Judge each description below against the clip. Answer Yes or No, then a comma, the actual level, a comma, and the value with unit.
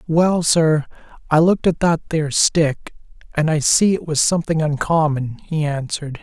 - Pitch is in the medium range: Yes, medium, 155 Hz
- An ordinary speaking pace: Yes, average, 165 wpm